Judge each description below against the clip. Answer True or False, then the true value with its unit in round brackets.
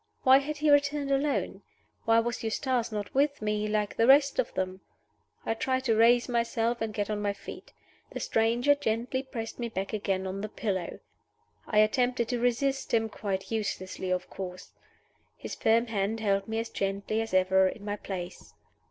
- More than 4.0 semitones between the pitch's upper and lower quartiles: False (3.6 semitones)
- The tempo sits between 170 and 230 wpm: True (180 wpm)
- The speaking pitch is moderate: False (225 Hz)